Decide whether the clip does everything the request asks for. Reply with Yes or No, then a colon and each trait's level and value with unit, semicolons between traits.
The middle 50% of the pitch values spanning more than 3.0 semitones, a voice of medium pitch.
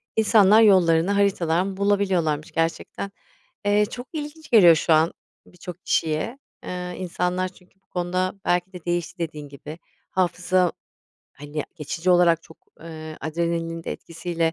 No: narrow, 2.5 semitones; medium, 175 Hz